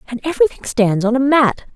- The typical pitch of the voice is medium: No, high, 245 Hz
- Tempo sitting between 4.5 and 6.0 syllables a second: No, 6.4 syllables/s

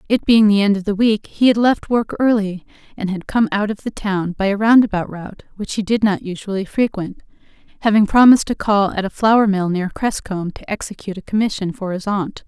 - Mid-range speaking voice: No, high, 205 Hz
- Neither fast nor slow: No, fast, 225 wpm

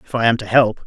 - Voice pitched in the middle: No, low, 115 Hz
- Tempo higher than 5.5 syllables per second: Yes, 6.5 syllables/s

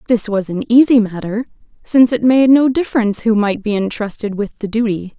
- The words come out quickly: No, average, 195 wpm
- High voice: Yes, high, 220 Hz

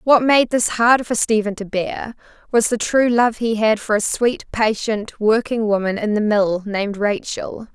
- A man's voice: No, female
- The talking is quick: No, average, 195 wpm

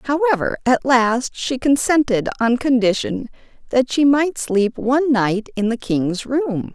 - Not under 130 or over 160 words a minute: Yes, average, 150 wpm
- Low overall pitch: No, very high, 250 Hz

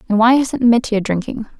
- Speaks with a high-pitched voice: Yes, high, 230 Hz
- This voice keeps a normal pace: Yes, average, 190 wpm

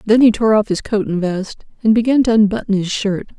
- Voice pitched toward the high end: Yes, high, 210 Hz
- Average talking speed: No, fast, 250 wpm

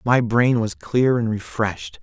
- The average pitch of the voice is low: Yes, low, 110 Hz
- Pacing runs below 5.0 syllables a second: Yes, 4.2 syllables/s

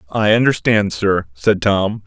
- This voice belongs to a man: Yes, male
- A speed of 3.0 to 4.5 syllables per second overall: Yes, 4.0 syllables/s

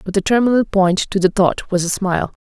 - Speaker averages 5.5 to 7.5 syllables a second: Yes, 5.8 syllables/s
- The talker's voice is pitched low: No, high, 195 Hz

